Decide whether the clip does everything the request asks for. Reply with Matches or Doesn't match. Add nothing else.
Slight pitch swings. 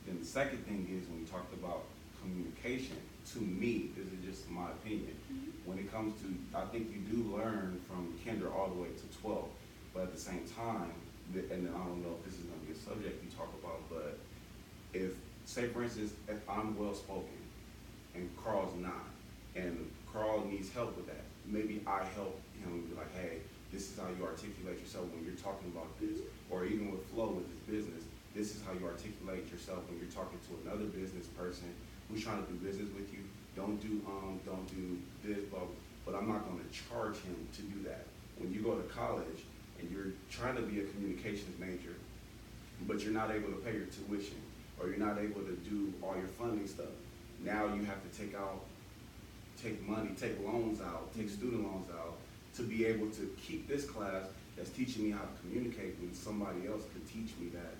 Doesn't match